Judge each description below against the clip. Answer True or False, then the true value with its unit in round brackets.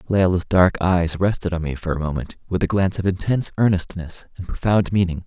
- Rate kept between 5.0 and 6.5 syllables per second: True (5.9 syllables/s)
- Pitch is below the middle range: True (90 Hz)